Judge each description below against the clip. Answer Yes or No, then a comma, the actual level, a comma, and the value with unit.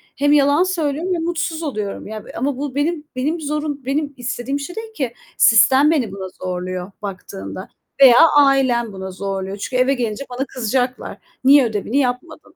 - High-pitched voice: Yes, very high, 265 Hz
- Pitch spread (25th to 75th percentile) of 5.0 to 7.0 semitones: Yes, wide, 5.4 semitones